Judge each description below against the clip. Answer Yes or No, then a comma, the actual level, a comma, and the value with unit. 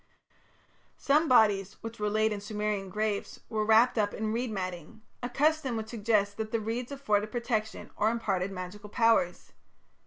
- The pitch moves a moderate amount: No, narrow, 2.2 semitones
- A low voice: No, high, 215 Hz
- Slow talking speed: No, average, 160 wpm